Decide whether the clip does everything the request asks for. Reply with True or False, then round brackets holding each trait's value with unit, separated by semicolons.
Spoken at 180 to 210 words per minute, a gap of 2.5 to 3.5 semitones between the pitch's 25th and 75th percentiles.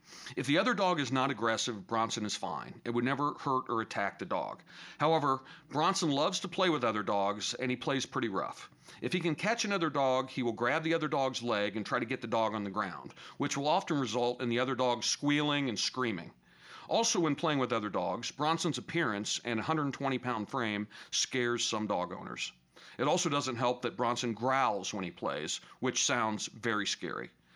False (205 wpm; 4.6 semitones)